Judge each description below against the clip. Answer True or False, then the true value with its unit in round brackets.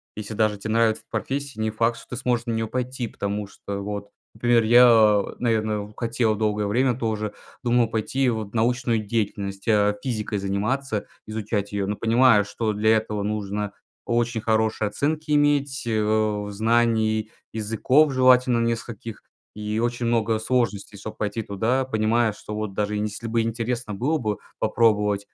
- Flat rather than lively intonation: True (2.2 semitones)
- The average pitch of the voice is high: False (110 Hz)